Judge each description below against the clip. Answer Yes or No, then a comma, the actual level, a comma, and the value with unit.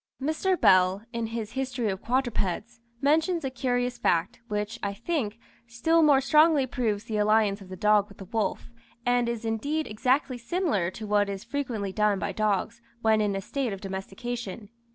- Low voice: No, high, 225 Hz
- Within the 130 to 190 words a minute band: Yes, average, 175 wpm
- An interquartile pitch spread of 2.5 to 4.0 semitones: No, average, 4.4 semitones